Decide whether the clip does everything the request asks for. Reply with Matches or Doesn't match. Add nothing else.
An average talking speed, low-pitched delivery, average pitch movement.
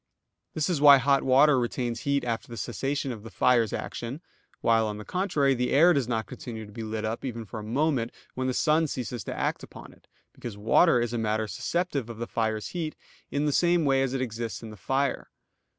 Doesn't match